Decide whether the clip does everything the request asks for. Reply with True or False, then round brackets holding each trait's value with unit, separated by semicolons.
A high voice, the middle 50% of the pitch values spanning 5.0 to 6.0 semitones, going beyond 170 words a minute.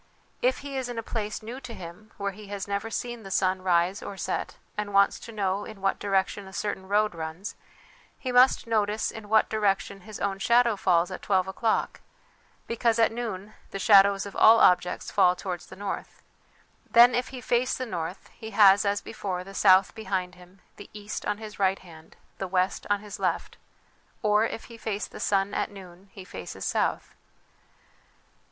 False (200 Hz; 2.6 semitones; 190 wpm)